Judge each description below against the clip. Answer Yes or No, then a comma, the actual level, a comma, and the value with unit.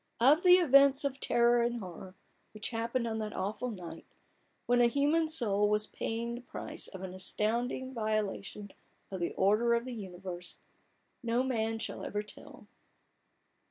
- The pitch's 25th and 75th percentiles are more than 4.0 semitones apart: No, average, 3.2 semitones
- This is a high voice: Yes, high, 230 Hz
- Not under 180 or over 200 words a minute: No, average, 160 wpm